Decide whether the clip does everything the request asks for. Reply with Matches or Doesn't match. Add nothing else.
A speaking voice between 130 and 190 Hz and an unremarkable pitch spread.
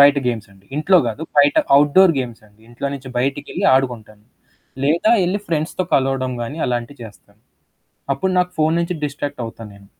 Matches